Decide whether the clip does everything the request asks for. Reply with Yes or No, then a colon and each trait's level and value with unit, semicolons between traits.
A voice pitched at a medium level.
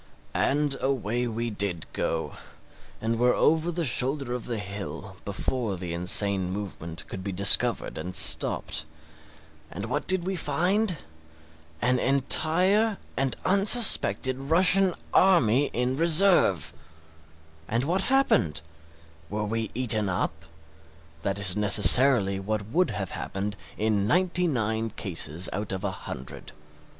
No: low, 115 Hz